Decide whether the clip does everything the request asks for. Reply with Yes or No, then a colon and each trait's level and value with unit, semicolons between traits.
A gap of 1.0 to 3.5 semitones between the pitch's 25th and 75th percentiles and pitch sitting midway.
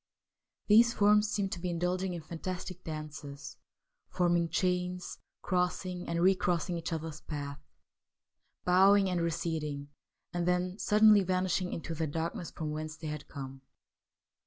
Yes: narrow, 2.6 semitones; medium, 175 Hz